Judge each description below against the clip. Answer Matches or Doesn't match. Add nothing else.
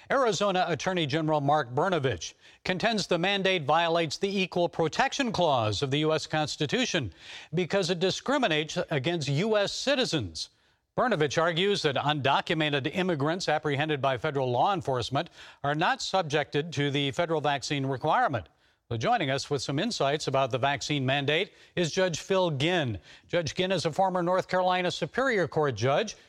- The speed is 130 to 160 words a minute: Matches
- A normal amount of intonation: Matches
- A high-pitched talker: Doesn't match